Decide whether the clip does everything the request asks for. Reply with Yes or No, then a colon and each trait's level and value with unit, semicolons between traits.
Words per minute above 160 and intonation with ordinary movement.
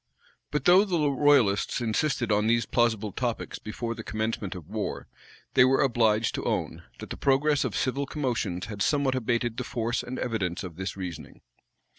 Yes: average, 175 wpm; average, 4.1 semitones